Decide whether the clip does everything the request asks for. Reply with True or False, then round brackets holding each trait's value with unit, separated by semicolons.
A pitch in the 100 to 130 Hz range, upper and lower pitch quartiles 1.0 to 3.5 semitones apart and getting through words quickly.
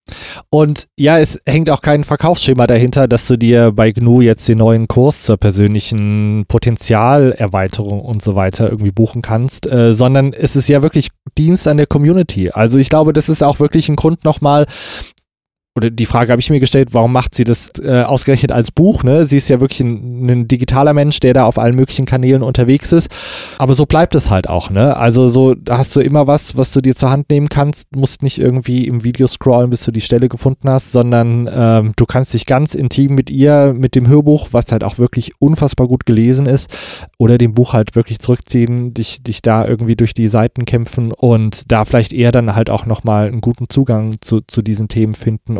True (125 Hz; 3.1 semitones; 210 wpm)